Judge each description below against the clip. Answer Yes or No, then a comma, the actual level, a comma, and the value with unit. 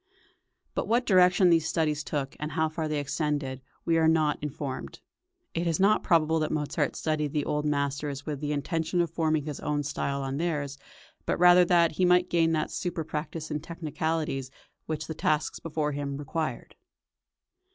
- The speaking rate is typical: Yes, average, 175 wpm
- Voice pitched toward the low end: No, medium, 155 Hz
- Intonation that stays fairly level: Yes, narrow, 2.1 semitones